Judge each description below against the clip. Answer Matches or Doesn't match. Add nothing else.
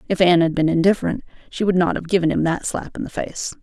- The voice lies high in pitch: Doesn't match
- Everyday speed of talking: Doesn't match